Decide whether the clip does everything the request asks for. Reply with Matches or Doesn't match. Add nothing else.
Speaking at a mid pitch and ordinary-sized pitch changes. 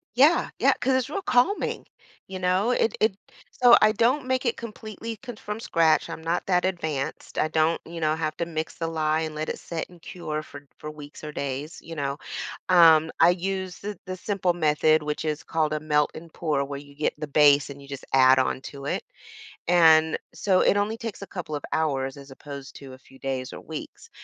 Matches